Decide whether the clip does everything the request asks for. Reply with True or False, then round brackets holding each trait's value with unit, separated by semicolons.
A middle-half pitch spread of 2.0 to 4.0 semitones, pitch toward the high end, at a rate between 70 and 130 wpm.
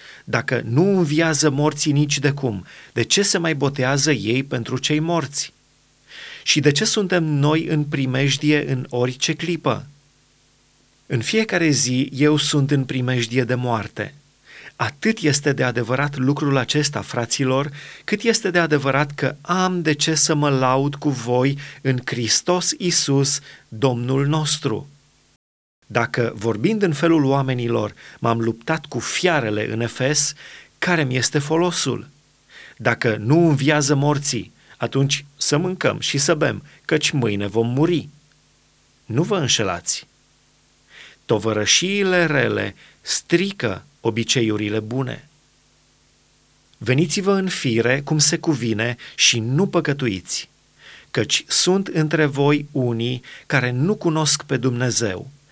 False (3.6 semitones; 140 Hz; 125 wpm)